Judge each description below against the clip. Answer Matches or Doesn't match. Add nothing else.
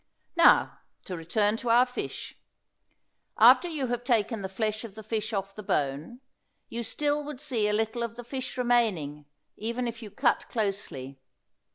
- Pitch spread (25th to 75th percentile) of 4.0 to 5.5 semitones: Doesn't match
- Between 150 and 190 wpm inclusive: Matches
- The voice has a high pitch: Matches